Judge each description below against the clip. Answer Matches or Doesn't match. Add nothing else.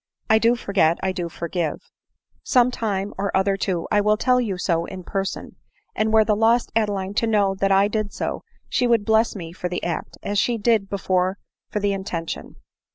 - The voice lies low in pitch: Doesn't match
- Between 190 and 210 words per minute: Matches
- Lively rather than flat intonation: Doesn't match